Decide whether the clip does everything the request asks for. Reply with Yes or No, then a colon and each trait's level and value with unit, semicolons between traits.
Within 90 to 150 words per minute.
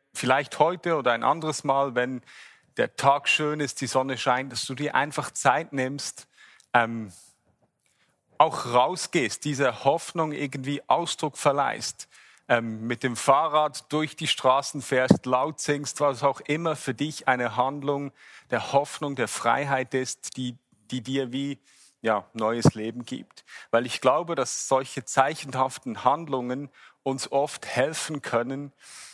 Yes: average, 140 wpm